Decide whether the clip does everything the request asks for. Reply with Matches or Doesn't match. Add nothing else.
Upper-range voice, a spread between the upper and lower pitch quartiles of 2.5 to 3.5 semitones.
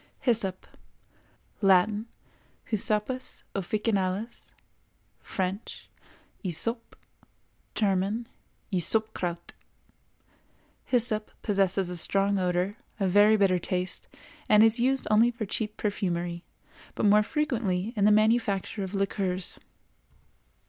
Matches